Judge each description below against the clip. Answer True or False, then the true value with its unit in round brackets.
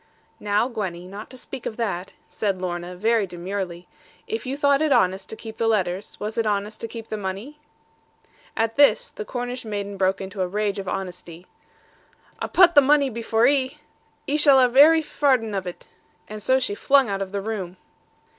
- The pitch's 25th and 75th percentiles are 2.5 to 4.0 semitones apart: False (5.3 semitones)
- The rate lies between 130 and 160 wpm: False (195 wpm)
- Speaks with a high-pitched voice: True (215 Hz)